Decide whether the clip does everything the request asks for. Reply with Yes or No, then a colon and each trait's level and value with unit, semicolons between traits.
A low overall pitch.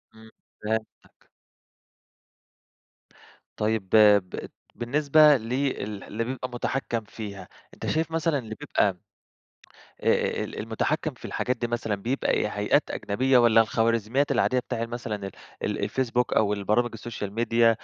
Yes: low, 115 Hz